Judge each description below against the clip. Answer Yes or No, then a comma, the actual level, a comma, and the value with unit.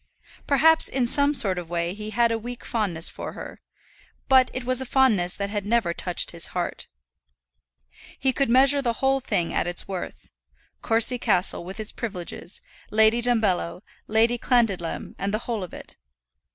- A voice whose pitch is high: Yes, high, 220 Hz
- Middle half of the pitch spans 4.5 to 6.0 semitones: Yes, average, 5.1 semitones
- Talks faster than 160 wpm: Yes, average, 170 wpm